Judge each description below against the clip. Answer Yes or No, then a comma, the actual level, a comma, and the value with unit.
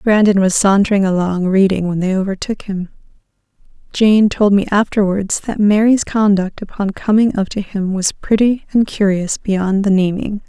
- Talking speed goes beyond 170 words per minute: No, average, 160 wpm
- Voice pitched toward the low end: No, high, 200 Hz